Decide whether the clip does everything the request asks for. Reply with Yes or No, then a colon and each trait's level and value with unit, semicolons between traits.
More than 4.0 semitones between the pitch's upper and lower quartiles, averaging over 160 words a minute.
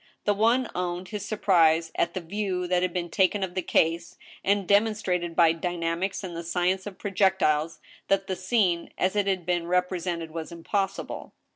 No: narrow, 2.5 semitones; average, 180 wpm